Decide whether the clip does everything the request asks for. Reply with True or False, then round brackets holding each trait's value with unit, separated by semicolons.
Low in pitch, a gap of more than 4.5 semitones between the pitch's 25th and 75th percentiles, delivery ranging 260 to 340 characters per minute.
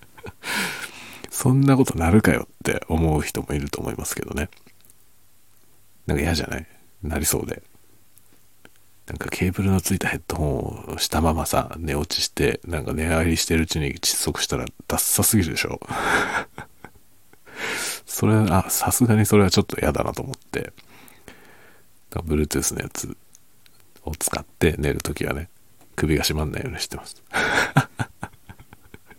True (90 Hz; 5.3 semitones; 310 characters per minute)